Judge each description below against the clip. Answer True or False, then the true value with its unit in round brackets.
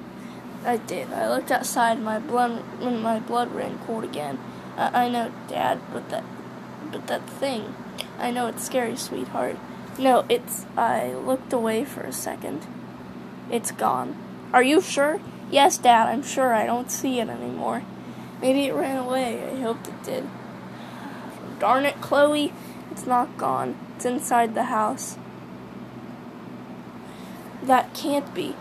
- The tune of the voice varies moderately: False (2.3 semitones)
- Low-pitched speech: False (245 Hz)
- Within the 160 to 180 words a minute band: False (145 wpm)